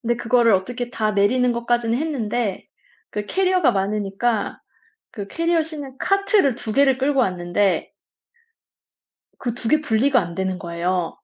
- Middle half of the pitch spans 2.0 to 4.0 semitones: No, average, 5.2 semitones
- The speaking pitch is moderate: No, high, 235 Hz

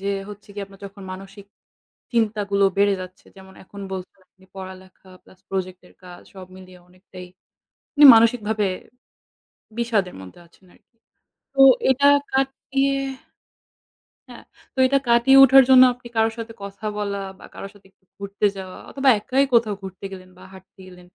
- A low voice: No, high, 200 Hz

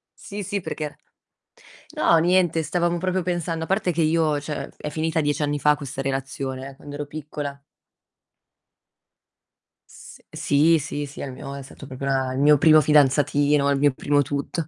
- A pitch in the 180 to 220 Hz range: No, medium, 145 Hz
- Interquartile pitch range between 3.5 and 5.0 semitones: No, narrow, 2.6 semitones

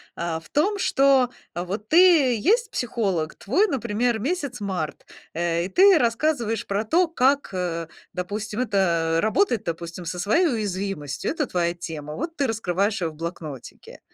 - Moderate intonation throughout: No, wide, 8.1 semitones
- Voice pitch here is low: No, high, 210 Hz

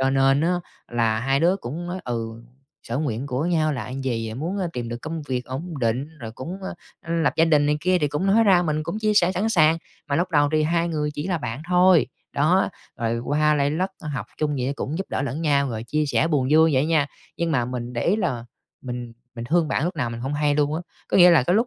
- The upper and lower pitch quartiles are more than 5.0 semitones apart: No, average, 4.7 semitones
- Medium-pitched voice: Yes, medium, 150 Hz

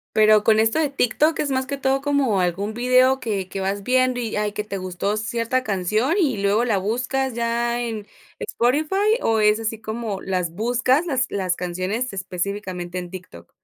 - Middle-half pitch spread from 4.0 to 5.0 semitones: Yes, average, 4.5 semitones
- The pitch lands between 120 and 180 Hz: No, high, 220 Hz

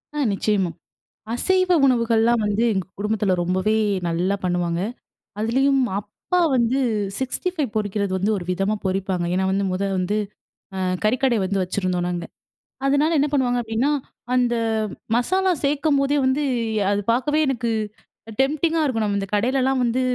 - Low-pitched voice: No, high, 225 Hz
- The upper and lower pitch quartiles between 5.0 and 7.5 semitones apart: Yes, wide, 5.5 semitones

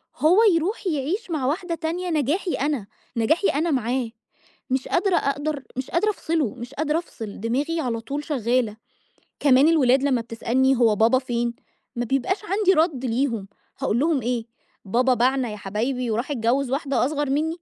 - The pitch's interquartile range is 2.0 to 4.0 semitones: No, average, 4.7 semitones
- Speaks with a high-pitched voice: Yes, very high, 270 Hz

